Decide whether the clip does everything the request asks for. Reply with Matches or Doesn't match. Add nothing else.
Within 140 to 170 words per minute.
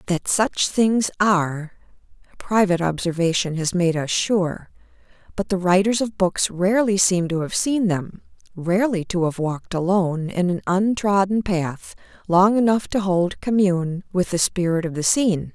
Matches